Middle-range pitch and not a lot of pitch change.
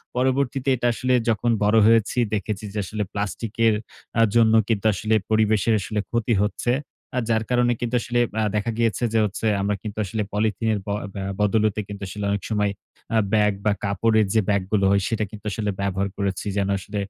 No: low, 110 Hz; narrow, 2.0 semitones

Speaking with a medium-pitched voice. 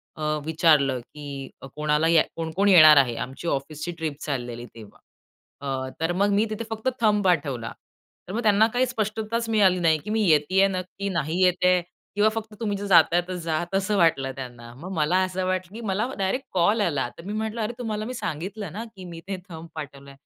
Yes: medium, 180 Hz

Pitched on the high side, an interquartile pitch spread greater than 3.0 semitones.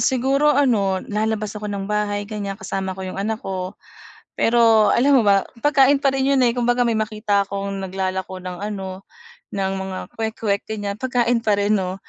Yes: high, 210 Hz; average, 3.4 semitones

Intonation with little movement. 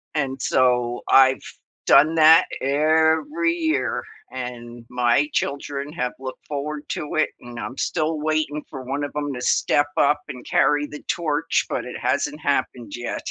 No: average, 3.6 semitones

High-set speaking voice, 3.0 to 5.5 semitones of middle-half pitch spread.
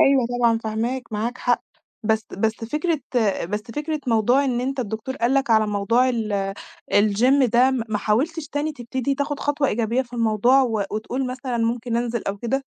Yes: high, 240 Hz; average, 3.3 semitones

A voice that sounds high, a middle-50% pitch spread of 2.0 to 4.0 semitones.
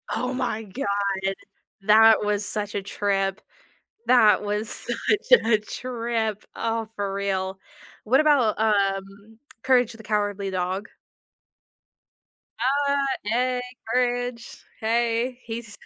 Yes: high, 220 Hz; average, 3.3 semitones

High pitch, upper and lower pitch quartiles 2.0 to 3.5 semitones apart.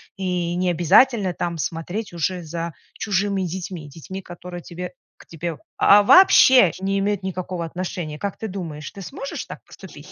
No: medium, 180 Hz; narrow, 2.5 semitones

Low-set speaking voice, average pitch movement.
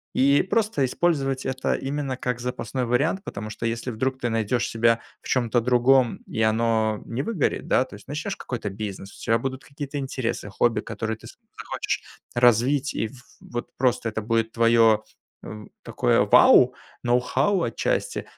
Yes: low, 125 Hz; average, 3.0 semitones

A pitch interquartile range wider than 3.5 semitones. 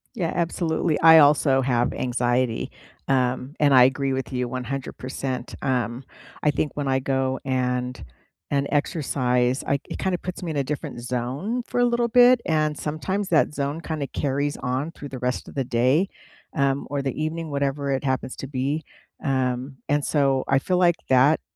No: average, 3.2 semitones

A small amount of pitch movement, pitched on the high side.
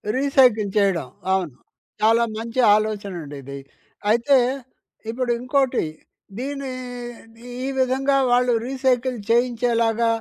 No: average, 3.3 semitones; high, 235 Hz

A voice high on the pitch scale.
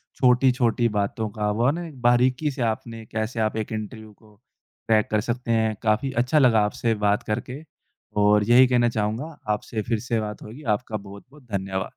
No: low, 115 Hz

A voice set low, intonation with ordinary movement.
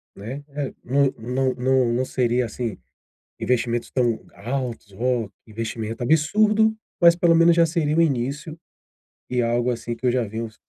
Yes: low, 125 Hz; average, 4.1 semitones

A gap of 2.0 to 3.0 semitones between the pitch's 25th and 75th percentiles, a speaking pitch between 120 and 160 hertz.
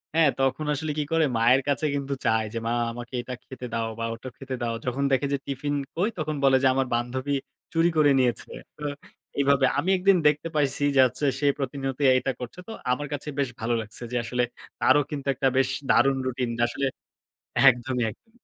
Yes: average, 2.7 semitones; low, 135 Hz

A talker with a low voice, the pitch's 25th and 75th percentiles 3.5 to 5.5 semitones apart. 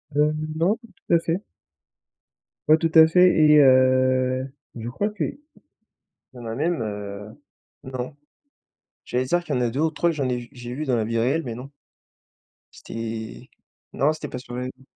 Yes: low, 130 Hz; average, 4.3 semitones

